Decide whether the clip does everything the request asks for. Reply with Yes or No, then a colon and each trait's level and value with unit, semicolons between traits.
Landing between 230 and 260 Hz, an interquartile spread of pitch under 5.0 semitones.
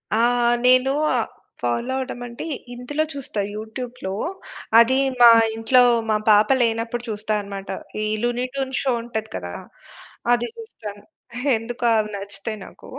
Yes: high, 235 Hz; average, 2.9 semitones